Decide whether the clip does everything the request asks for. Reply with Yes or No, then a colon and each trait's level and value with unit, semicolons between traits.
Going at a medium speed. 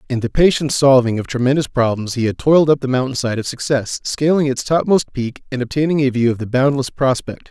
No: fast, 215 wpm